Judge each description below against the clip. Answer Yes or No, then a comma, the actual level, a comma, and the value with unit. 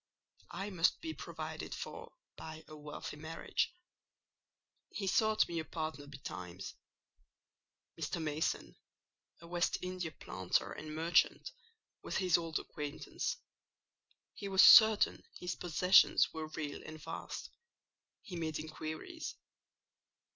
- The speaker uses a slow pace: Yes, slow, 115 wpm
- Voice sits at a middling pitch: Yes, medium, 160 Hz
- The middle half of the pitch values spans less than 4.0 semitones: Yes, average, 3.0 semitones